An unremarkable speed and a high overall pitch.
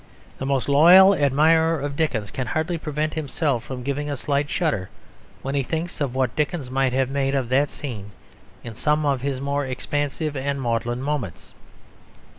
No: average, 175 wpm; medium, 140 Hz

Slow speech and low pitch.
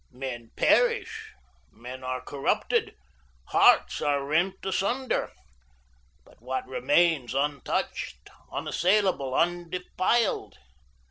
No: slow, 80 wpm; medium, 150 Hz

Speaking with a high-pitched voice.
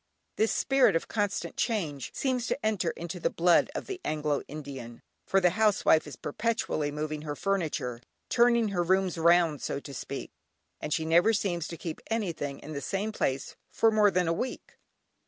No: medium, 175 Hz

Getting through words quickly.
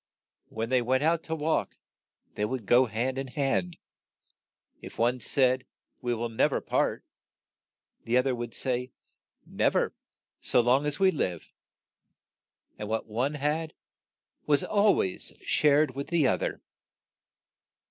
No: average, 145 wpm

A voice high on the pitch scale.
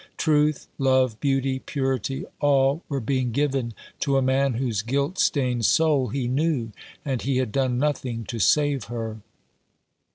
No: low, 135 Hz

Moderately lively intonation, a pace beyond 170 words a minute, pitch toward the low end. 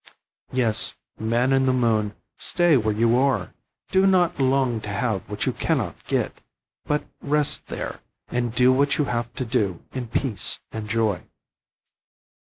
No: average, 3.6 semitones; average, 160 wpm; low, 120 Hz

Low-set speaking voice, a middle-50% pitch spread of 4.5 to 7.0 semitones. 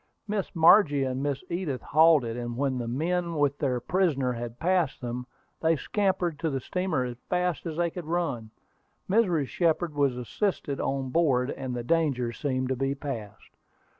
No: medium, 145 Hz; average, 5.1 semitones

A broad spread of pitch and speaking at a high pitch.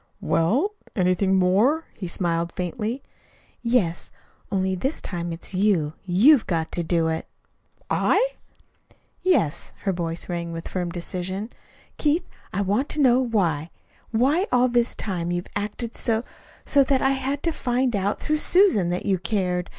Yes: wide, 6.3 semitones; high, 200 Hz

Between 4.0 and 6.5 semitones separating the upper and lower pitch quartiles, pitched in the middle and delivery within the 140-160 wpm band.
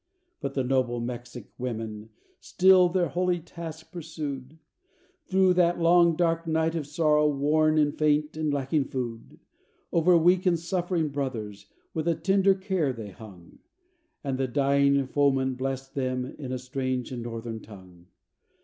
Yes: average, 4.7 semitones; medium, 145 Hz; average, 150 wpm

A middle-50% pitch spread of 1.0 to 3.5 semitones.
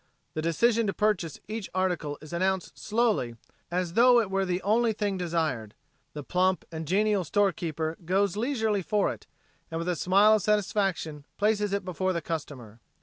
No: average, 4.1 semitones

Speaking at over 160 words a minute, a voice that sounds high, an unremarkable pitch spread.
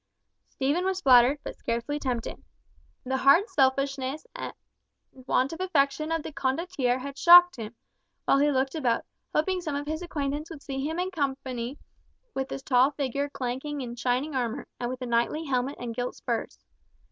Yes: average, 170 wpm; very high, 275 Hz; average, 3.2 semitones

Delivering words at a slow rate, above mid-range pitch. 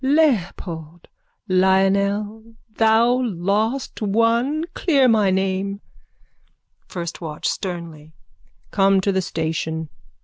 Yes: slow, 90 wpm; high, 195 Hz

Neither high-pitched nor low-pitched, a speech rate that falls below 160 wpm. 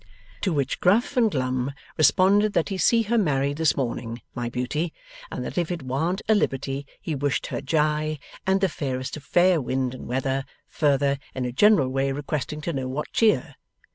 No: medium, 145 Hz; average, 190 wpm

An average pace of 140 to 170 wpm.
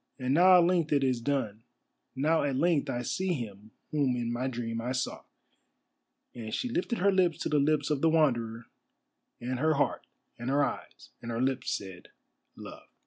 No: average, 190 wpm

